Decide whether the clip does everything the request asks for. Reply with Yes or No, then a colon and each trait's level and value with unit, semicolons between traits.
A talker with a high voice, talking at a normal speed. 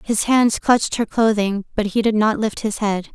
No: high, 215 Hz; fast, 230 wpm